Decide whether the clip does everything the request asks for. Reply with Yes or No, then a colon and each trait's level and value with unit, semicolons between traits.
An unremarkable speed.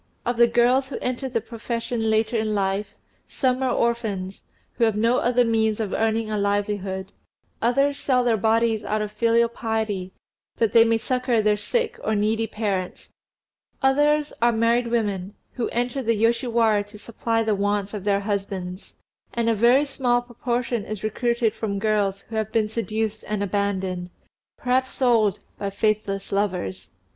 Yes: average, 165 wpm